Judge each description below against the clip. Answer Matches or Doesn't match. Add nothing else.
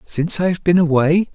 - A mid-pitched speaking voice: Matches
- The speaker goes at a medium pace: Matches